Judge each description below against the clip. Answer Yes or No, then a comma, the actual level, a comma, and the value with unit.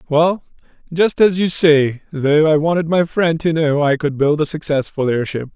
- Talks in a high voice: No, medium, 155 Hz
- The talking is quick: No, average, 195 wpm